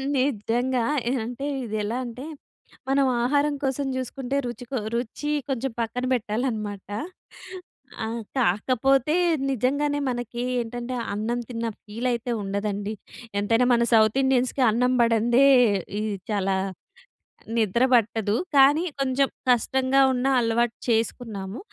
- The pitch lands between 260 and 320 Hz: No, high, 240 Hz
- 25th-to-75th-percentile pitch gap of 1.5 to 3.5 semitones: Yes, average, 2.9 semitones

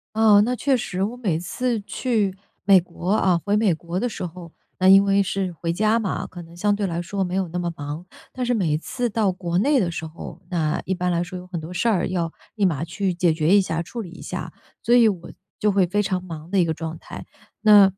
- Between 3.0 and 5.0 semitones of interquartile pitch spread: Yes, average, 3.3 semitones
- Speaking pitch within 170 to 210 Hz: Yes, medium, 185 Hz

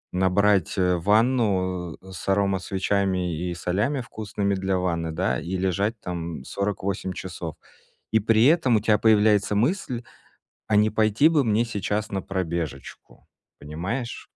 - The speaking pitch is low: Yes, low, 100 Hz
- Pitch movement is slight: No, average, 3.0 semitones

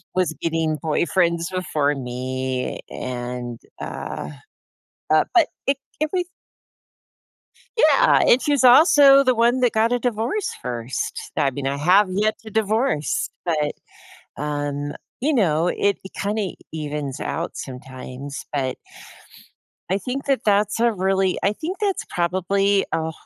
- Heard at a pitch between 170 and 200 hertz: Yes, medium, 185 Hz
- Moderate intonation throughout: No, wide, 8.1 semitones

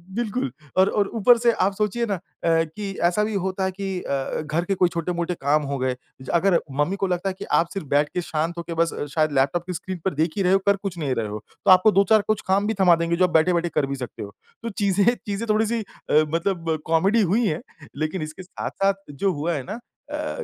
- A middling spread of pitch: Yes, average, 4.0 semitones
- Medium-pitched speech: Yes, medium, 180 Hz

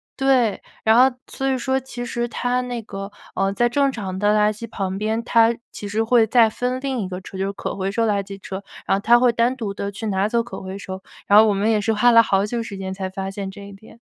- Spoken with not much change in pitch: No, average, 3.4 semitones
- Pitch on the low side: No, high, 215 Hz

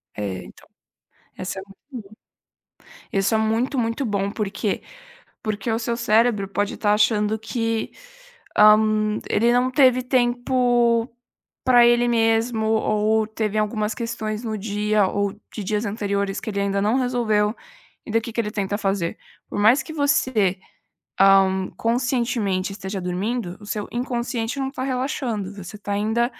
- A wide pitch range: No, average, 2.8 semitones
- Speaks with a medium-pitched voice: No, high, 220 Hz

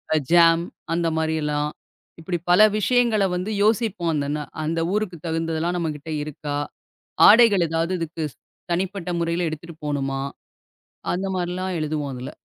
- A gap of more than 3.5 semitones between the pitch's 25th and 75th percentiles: No, average, 3.1 semitones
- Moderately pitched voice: Yes, medium, 170 Hz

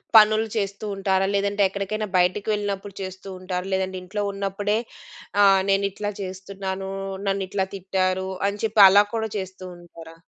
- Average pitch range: No, narrow, 1.3 semitones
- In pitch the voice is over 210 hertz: No, high, 195 Hz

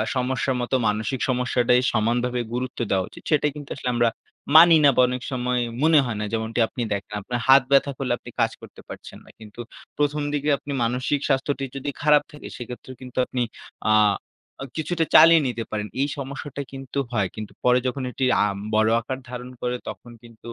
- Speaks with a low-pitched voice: Yes, low, 125 Hz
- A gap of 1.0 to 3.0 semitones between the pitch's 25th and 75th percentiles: Yes, narrow, 2.6 semitones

